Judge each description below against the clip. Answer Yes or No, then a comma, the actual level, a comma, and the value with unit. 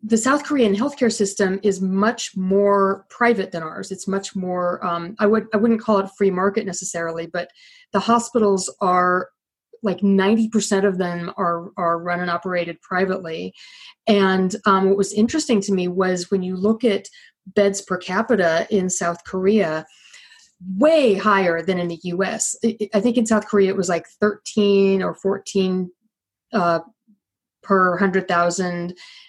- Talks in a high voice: Yes, high, 195 Hz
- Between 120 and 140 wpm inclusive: No, average, 155 wpm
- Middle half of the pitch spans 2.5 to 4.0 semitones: Yes, average, 2.8 semitones